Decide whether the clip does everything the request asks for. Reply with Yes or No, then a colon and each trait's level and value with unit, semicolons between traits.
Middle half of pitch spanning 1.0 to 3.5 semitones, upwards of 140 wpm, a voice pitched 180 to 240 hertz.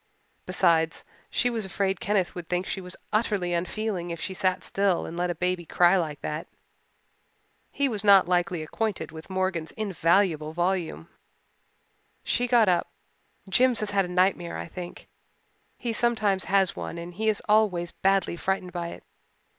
Yes: average, 2.8 semitones; average, 160 wpm; medium, 185 Hz